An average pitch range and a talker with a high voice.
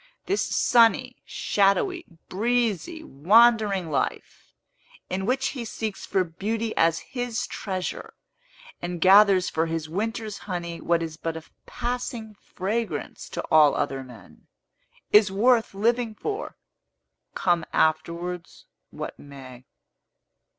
No: wide, 5.7 semitones; high, 200 Hz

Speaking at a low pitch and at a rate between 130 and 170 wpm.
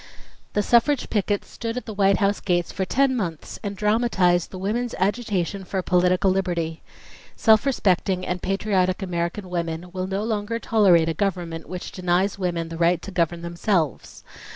No: high, 190 Hz; average, 165 wpm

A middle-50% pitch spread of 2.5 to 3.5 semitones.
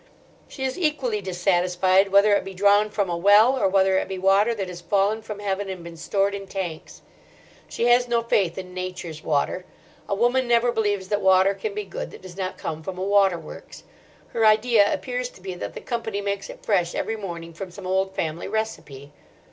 Yes: average, 2.9 semitones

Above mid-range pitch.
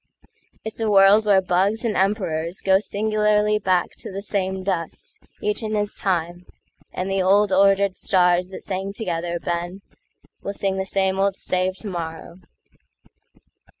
Yes: high, 195 Hz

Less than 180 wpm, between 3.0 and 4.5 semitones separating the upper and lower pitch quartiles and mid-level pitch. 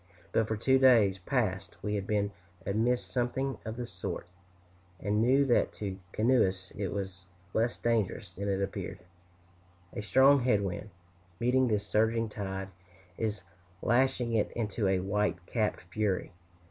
No: average, 150 wpm; average, 3.5 semitones; low, 105 Hz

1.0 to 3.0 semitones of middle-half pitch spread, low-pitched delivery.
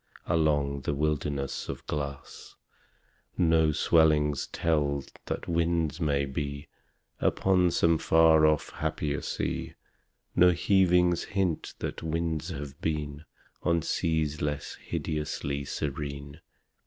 Yes: narrow, 2.4 semitones; very low, 75 Hz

